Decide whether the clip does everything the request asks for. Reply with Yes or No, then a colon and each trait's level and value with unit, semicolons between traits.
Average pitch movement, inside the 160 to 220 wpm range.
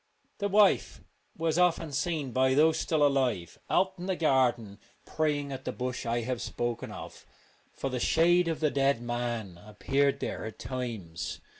Yes: average, 5.0 semitones; average, 165 wpm